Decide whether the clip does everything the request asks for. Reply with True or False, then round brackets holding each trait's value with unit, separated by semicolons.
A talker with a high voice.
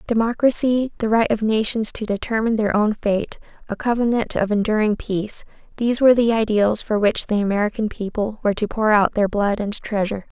True (215 Hz)